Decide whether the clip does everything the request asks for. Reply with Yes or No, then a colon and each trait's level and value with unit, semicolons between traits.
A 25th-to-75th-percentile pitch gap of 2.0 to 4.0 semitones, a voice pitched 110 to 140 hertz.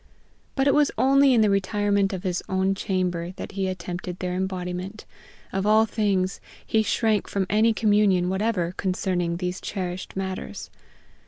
No: narrow, 2.6 semitones; high, 190 Hz